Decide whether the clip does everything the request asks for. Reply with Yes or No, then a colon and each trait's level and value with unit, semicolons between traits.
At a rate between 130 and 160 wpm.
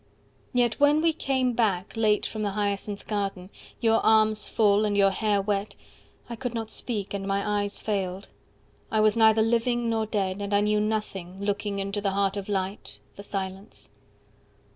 No: average, 180 wpm